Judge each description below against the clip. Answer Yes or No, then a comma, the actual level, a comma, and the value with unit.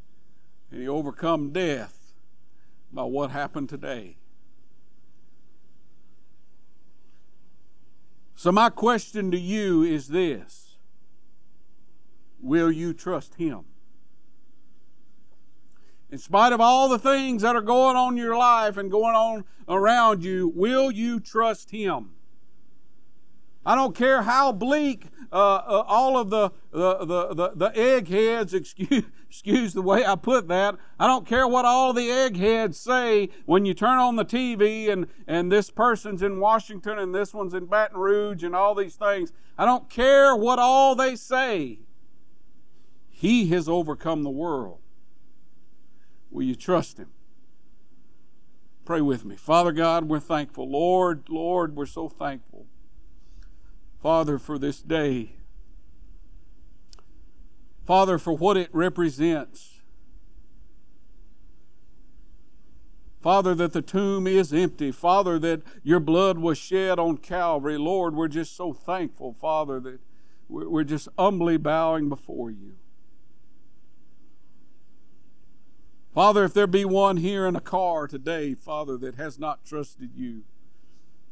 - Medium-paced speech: No, slow, 130 wpm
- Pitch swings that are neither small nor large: No, wide, 6.3 semitones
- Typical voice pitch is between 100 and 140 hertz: No, medium, 180 Hz